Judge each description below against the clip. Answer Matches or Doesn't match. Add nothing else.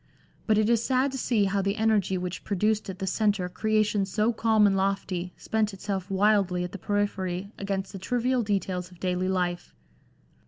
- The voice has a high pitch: Matches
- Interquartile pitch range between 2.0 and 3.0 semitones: Matches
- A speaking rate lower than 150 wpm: Doesn't match